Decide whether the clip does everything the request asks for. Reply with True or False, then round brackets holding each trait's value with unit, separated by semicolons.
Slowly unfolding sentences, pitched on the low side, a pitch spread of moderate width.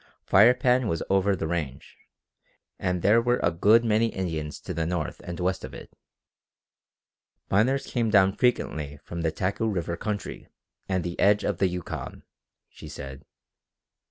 False (155 wpm; 95 Hz; 4.4 semitones)